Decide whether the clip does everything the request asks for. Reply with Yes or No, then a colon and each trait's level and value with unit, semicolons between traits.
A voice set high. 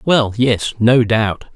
No: low, 115 Hz